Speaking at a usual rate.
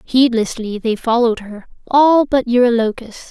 No: slow, 125 wpm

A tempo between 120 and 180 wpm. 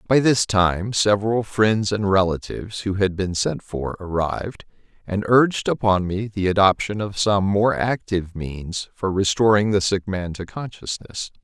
Yes: average, 165 wpm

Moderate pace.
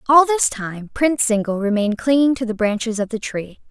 No: fast, 210 wpm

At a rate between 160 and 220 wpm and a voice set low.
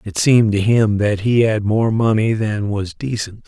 Yes: fast, 205 wpm; low, 110 Hz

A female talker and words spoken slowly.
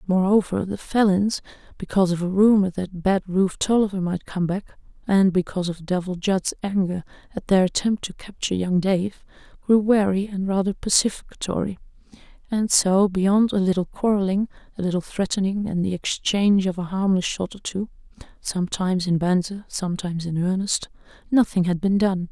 No: female; average, 160 wpm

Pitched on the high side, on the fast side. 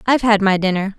Yes: high, 205 Hz; fast, 245 wpm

